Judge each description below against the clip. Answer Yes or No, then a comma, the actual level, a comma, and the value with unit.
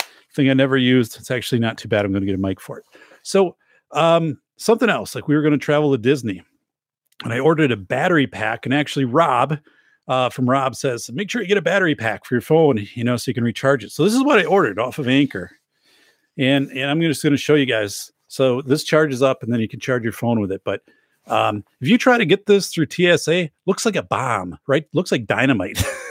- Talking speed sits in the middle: No, fast, 245 wpm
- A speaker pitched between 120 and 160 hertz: Yes, low, 135 Hz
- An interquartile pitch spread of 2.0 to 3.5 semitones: No, average, 5.2 semitones